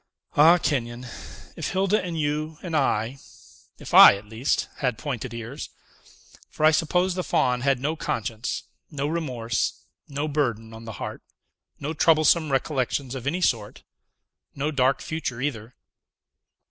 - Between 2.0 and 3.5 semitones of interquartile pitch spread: No, average, 4.7 semitones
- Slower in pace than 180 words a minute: Yes, average, 145 wpm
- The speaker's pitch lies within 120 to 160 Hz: Yes, medium, 140 Hz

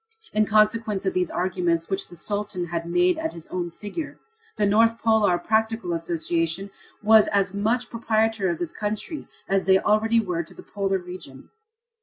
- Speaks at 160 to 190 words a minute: Yes, average, 170 wpm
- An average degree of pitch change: Yes, average, 3.9 semitones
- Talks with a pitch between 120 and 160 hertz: No, high, 200 Hz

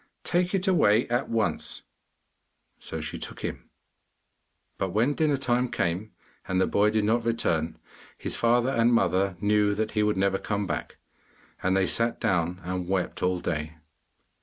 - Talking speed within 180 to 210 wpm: No, average, 160 wpm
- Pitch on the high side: No, low, 105 Hz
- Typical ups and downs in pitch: Yes, average, 4.2 semitones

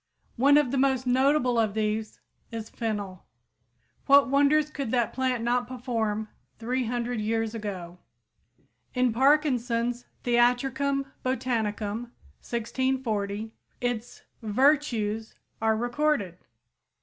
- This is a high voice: Yes, high, 240 Hz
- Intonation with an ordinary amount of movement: Yes, average, 3.0 semitones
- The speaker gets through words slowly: Yes, slow, 100 wpm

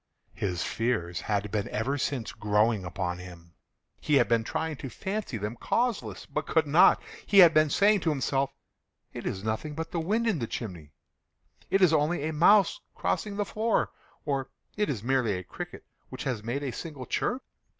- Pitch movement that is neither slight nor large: No, wide, 7.5 semitones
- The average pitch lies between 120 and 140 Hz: Yes, low, 135 Hz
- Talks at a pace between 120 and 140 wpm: No, average, 180 wpm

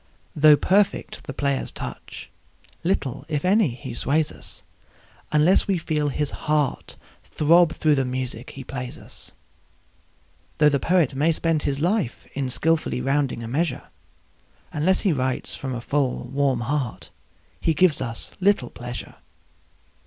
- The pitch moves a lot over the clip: No, average, 3.8 semitones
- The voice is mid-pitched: Yes, medium, 145 Hz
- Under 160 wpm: Yes, average, 145 wpm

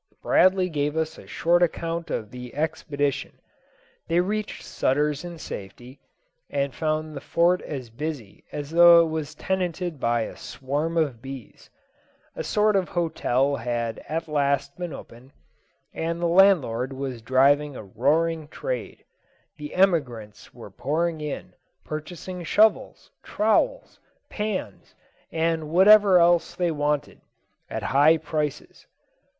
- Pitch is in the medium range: Yes, medium, 155 Hz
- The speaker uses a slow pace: Yes, slow, 130 wpm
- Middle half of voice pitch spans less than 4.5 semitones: Yes, average, 3.9 semitones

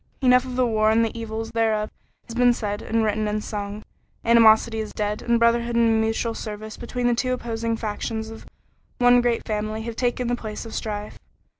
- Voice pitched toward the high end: Yes, high, 225 Hz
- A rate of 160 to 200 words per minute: Yes, average, 195 wpm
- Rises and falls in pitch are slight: Yes, narrow, 1.6 semitones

